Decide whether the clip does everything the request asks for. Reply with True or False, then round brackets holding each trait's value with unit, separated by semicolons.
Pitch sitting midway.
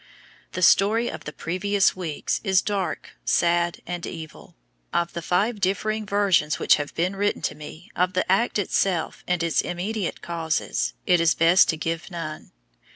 True (180 Hz)